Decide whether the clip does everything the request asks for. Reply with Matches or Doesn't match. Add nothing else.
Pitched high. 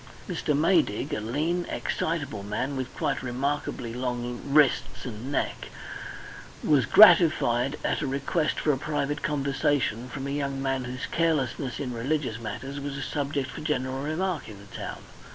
Doesn't match